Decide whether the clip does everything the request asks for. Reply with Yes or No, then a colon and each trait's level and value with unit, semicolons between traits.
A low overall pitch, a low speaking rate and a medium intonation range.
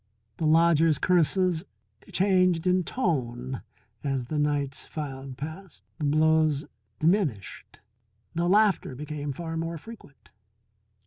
No: medium, 155 Hz; slow, 110 wpm; average, 3.8 semitones